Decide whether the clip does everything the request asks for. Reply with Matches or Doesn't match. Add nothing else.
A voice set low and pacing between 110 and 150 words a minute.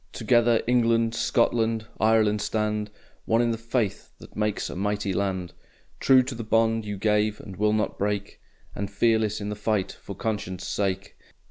Doesn't match